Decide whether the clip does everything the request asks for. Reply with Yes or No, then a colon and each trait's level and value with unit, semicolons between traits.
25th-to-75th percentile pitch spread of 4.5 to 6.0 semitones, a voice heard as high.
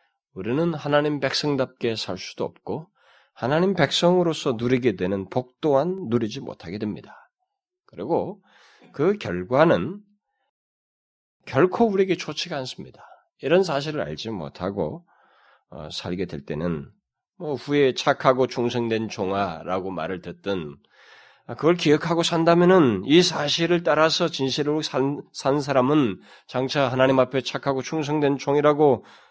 No: wide, 5.6 semitones; medium, 140 Hz